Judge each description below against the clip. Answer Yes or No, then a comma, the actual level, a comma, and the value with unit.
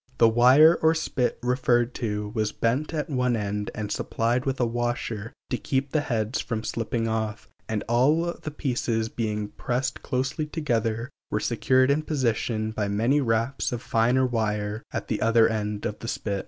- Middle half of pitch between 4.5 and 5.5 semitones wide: No, average, 3.1 semitones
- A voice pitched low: Yes, low, 120 Hz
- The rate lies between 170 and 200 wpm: Yes, average, 175 wpm